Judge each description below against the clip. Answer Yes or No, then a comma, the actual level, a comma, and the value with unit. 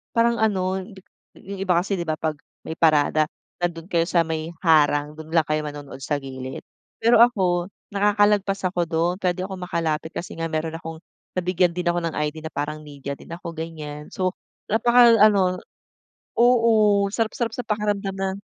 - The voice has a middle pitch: Yes, medium, 175 Hz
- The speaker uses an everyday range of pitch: Yes, average, 4.2 semitones